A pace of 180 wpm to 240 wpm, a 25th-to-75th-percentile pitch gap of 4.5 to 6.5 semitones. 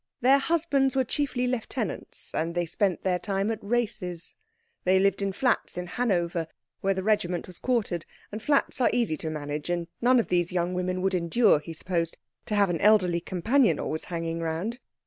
Yes: average, 185 wpm; average, 5.3 semitones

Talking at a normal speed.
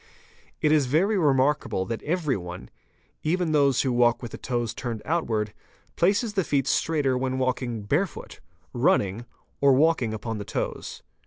Yes: average, 150 wpm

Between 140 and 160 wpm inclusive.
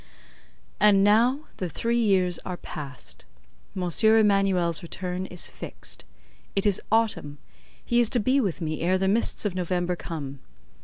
Yes: average, 150 wpm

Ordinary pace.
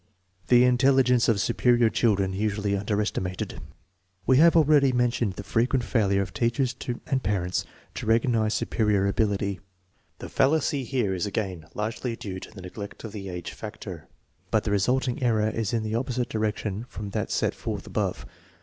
Yes: average, 170 wpm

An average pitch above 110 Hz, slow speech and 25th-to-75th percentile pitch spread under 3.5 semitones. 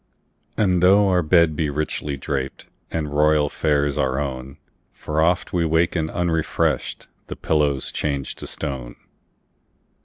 No: very low, 75 Hz; slow, 115 wpm; average, 2.8 semitones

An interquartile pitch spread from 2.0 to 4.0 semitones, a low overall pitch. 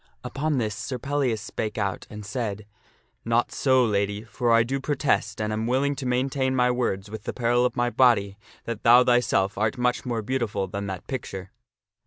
Yes: average, 3.4 semitones; low, 120 Hz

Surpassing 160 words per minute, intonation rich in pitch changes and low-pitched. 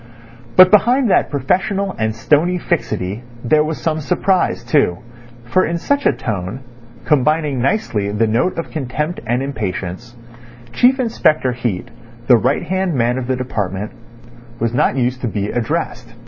No: average, 150 wpm; wide, 6.7 semitones; low, 130 Hz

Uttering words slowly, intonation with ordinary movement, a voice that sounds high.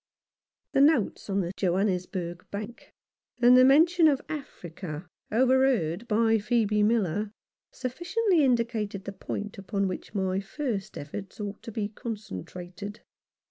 Yes: slow, 125 wpm; average, 4.6 semitones; high, 210 Hz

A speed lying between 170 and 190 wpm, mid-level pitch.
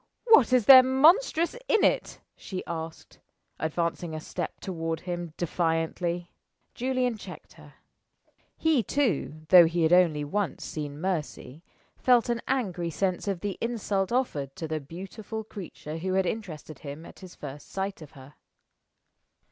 No: average, 150 wpm; medium, 180 Hz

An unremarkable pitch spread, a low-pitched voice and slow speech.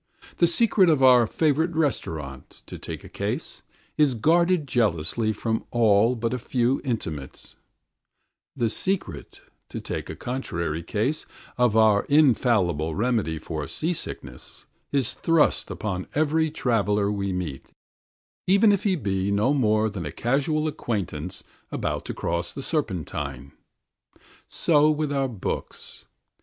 No: wide, 7.6 semitones; low, 120 Hz; slow, 130 wpm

